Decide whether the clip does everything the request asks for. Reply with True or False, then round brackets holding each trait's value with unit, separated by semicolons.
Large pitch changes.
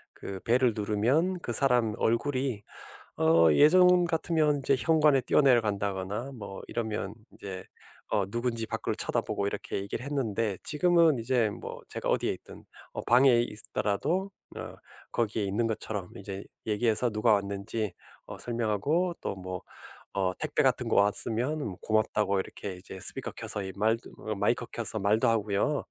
False (4.8 semitones)